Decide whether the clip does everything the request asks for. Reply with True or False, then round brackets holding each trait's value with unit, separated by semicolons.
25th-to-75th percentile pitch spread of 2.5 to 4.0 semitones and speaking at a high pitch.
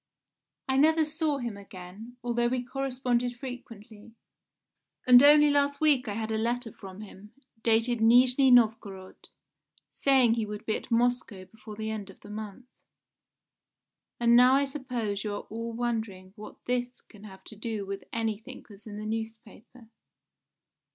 True (2.9 semitones; 230 Hz)